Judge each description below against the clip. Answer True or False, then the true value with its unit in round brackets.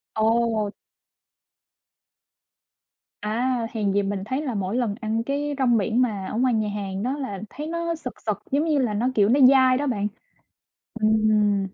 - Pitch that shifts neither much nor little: True (3.9 semitones)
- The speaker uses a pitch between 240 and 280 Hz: False (225 Hz)